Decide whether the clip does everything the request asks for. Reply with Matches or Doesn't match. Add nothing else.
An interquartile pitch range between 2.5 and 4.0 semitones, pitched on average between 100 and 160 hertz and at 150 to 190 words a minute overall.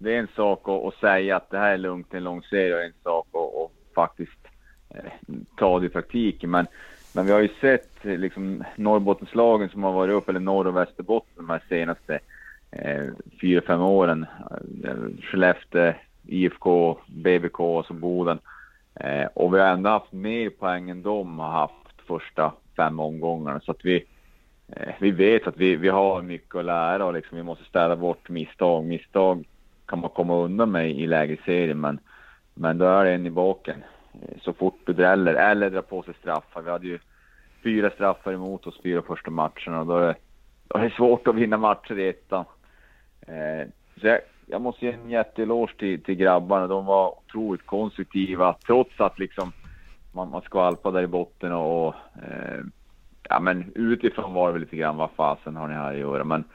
Doesn't match